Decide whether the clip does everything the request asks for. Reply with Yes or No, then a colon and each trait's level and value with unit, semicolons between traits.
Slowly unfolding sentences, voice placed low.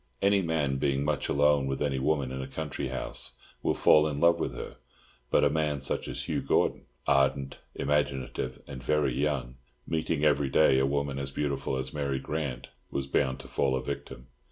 No: average, 190 wpm; very low, 70 Hz